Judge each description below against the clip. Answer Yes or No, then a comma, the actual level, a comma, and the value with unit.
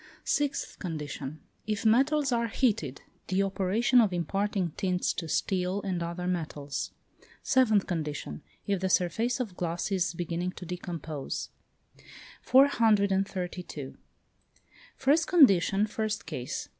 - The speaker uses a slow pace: Yes, slow, 115 wpm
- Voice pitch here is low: No, high, 190 Hz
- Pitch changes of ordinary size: Yes, average, 4.3 semitones